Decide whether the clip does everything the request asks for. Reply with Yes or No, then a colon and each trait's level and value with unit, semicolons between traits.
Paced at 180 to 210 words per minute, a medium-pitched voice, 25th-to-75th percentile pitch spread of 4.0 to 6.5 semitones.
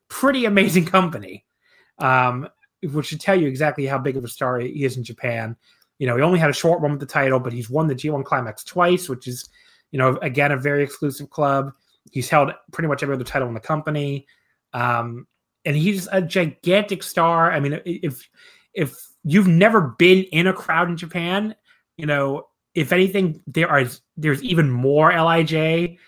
Yes: average, 190 wpm; medium, 150 Hz; average, 4.4 semitones